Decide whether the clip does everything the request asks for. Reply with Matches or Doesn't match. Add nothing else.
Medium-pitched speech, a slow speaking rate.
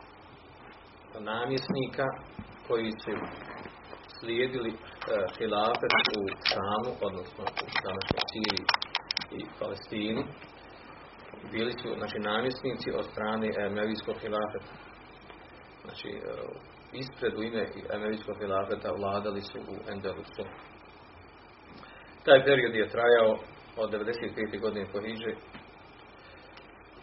Doesn't match